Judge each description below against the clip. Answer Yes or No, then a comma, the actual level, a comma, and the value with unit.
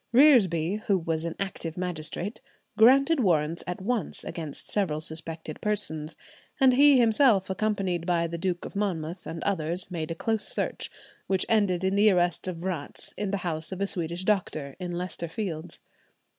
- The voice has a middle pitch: Yes, medium, 180 Hz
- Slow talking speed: No, average, 170 wpm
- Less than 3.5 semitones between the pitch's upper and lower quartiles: No, average, 3.8 semitones